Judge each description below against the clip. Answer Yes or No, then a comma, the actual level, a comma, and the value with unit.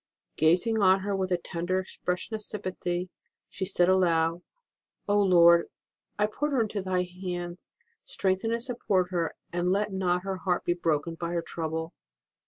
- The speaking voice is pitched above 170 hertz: Yes, medium, 185 Hz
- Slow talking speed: No, average, 170 wpm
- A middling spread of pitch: No, narrow, 2.0 semitones